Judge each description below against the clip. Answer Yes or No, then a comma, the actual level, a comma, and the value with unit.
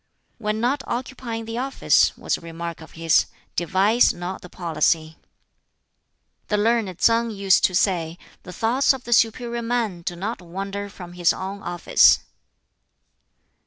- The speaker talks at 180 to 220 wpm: No, average, 145 wpm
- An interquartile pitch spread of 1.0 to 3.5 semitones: No, average, 4.9 semitones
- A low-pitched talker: No, high, 200 Hz